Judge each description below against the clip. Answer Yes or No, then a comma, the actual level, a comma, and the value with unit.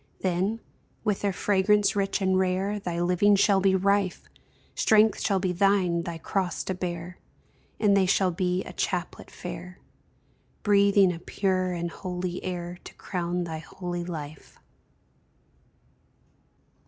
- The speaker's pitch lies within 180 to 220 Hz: Yes, medium, 185 Hz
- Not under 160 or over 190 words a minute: No, slow, 135 wpm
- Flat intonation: Yes, narrow, 2.1 semitones